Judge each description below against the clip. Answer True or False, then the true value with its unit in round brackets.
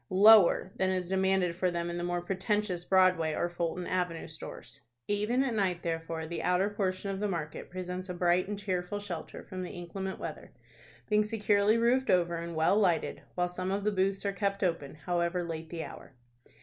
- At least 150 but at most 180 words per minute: False (195 wpm)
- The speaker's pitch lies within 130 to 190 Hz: True (185 Hz)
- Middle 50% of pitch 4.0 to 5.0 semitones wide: False (2.5 semitones)